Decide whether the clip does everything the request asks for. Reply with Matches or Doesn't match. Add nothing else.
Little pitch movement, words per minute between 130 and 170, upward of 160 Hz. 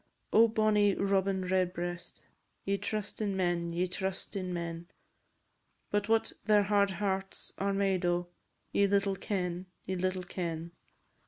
Matches